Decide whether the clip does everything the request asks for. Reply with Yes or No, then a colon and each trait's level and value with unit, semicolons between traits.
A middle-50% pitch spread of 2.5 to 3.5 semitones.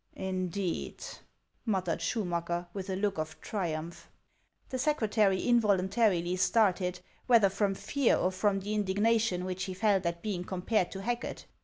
Yes: average, 3.0 semitones